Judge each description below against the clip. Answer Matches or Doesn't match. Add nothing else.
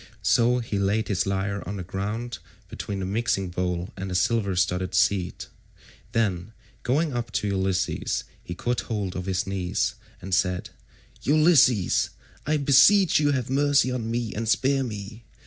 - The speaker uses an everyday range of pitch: Matches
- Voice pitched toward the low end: Matches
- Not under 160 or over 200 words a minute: Matches